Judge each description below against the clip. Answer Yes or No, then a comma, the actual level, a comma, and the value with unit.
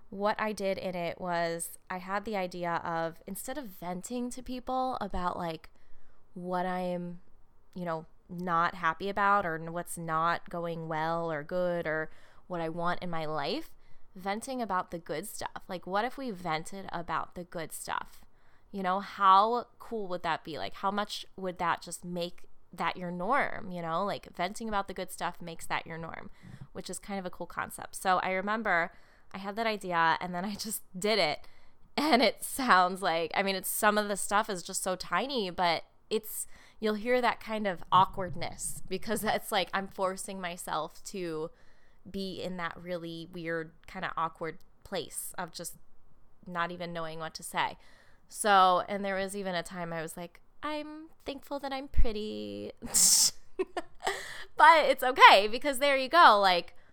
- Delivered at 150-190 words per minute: Yes, average, 180 wpm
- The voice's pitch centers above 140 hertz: Yes, medium, 185 Hz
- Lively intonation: No, average, 3.3 semitones